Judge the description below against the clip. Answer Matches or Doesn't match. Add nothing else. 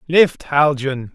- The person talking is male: Matches